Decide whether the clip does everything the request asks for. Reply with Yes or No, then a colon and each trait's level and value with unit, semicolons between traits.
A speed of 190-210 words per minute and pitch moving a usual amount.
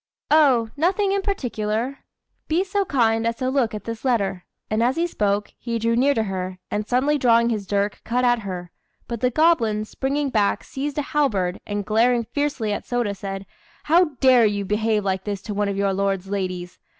Yes: average, 200 wpm; average, 4.8 semitones